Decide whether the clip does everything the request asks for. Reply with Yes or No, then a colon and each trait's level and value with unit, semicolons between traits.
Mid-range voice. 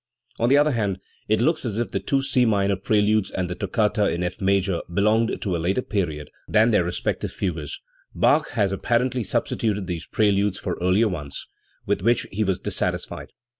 No: low, 100 Hz